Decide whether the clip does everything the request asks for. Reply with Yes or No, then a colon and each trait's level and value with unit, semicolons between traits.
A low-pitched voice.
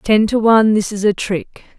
No: high, 210 Hz